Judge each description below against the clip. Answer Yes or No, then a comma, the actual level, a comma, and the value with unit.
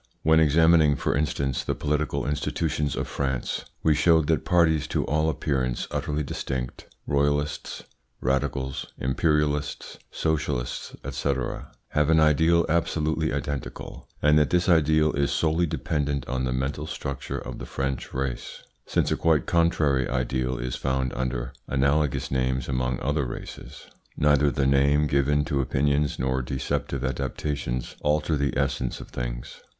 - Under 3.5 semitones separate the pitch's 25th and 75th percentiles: Yes, narrow, 2.6 semitones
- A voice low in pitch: Yes, very low, 70 Hz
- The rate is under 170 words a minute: Yes, average, 140 wpm